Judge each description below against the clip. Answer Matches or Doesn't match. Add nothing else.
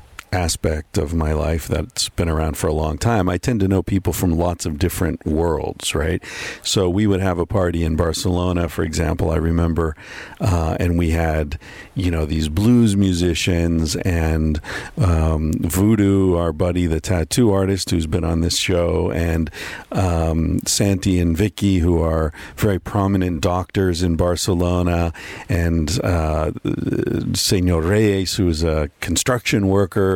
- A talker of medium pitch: Doesn't match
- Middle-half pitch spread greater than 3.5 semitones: Doesn't match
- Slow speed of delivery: Doesn't match